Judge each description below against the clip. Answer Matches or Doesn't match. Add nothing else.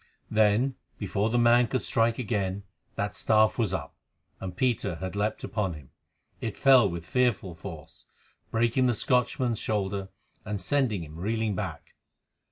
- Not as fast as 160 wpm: Matches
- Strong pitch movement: Doesn't match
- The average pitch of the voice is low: Matches